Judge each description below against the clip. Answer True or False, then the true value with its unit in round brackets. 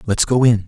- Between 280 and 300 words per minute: False (270 wpm)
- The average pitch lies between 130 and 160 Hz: False (115 Hz)